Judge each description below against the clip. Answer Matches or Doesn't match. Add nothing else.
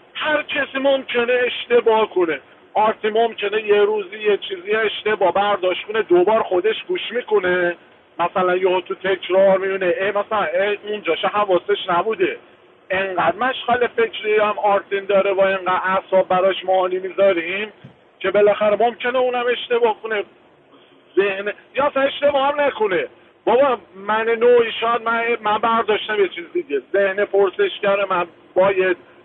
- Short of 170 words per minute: Matches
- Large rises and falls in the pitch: Matches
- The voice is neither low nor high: Doesn't match